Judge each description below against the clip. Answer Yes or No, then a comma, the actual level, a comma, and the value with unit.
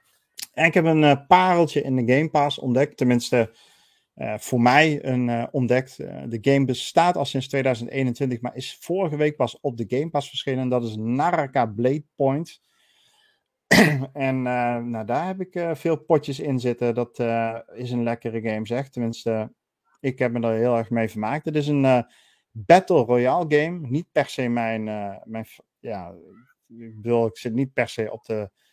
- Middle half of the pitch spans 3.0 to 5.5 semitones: Yes, average, 3.5 semitones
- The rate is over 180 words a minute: Yes, average, 190 wpm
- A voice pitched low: Yes, low, 130 Hz